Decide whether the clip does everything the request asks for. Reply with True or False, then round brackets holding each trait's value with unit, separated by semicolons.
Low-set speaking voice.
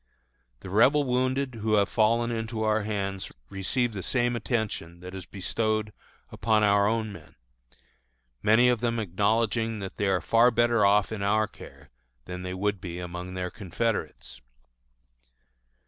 True (105 Hz)